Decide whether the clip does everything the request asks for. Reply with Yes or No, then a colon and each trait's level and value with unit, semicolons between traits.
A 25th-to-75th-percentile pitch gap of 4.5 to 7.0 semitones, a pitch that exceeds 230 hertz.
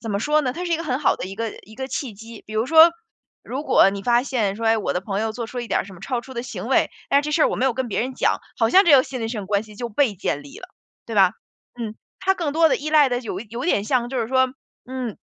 No: average, 3.7 semitones; high, 240 Hz